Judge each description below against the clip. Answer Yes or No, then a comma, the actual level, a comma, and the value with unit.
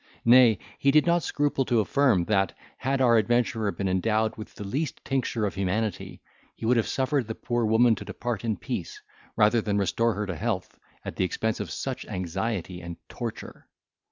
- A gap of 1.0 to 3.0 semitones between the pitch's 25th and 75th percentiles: No, average, 3.5 semitones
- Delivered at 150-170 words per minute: No, average, 185 wpm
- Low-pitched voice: Yes, low, 110 Hz